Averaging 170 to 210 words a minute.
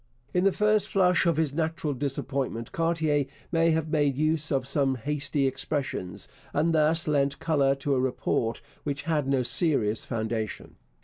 No: average, 160 wpm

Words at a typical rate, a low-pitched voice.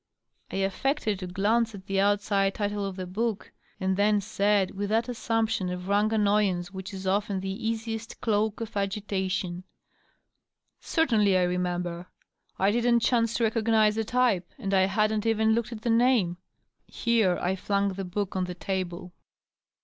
No: average, 165 wpm; high, 205 Hz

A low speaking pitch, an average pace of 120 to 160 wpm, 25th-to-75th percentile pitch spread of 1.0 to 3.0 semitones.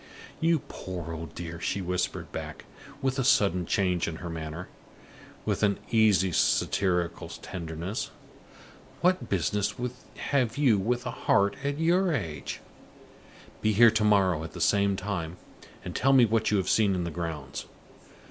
No: very low, 95 Hz; average, 155 wpm; average, 4.8 semitones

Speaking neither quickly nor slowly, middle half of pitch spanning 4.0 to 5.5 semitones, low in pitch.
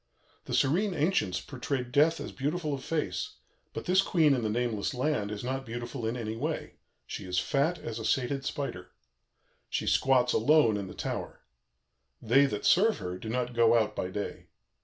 Yes: average, 180 wpm; average, 5.0 semitones; low, 125 Hz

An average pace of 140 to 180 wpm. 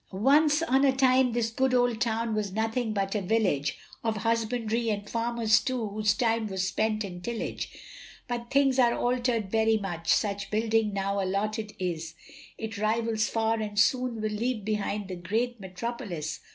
Yes: average, 165 wpm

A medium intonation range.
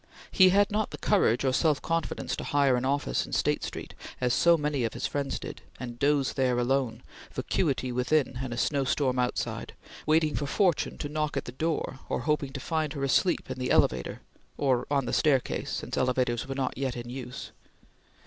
Yes: average, 3.1 semitones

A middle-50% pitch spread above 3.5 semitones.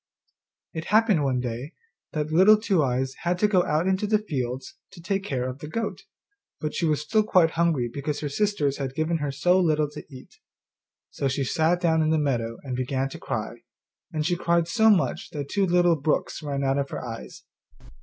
Yes: average, 4.6 semitones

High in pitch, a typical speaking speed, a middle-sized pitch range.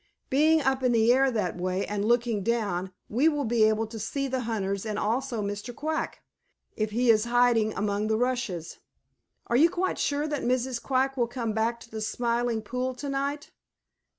Yes: high, 235 Hz; average, 190 wpm; average, 3.4 semitones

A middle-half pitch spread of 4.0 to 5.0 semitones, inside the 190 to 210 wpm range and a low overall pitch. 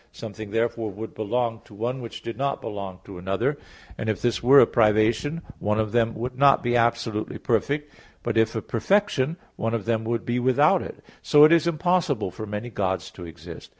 No: average, 3.5 semitones; average, 200 wpm; low, 115 Hz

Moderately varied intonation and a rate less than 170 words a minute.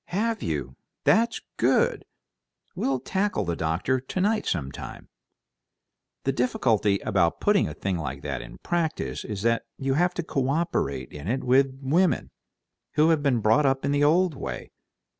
No: wide, 8.8 semitones; average, 160 wpm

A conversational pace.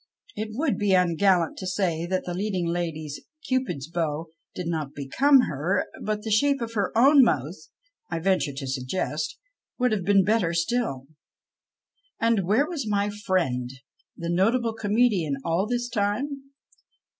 Yes: average, 155 wpm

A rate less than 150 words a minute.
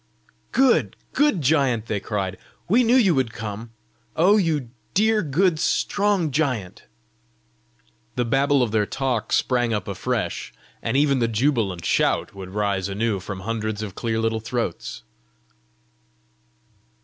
Yes: slow, 135 wpm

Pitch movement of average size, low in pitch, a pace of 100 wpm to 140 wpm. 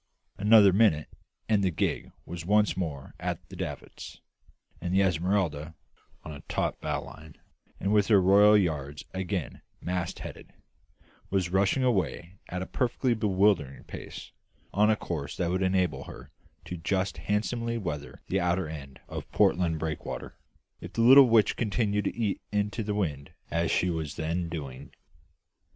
No: average, 4.3 semitones; very low, 95 Hz; average, 155 wpm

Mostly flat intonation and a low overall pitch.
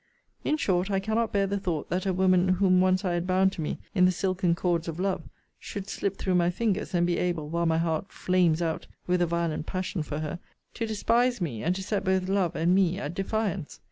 No: narrow, 2.3 semitones; medium, 185 Hz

